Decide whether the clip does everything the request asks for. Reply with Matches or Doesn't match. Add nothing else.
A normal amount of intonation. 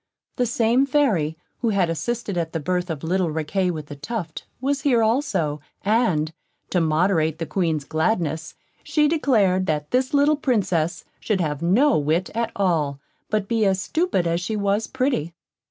Doesn't match